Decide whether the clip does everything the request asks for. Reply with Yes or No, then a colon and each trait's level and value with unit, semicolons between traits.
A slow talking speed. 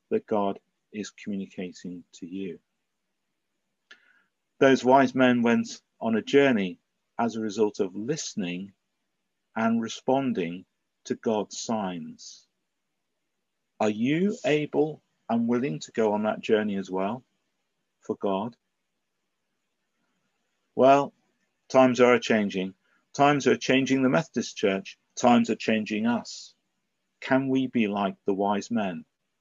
Yes: slow, 120 wpm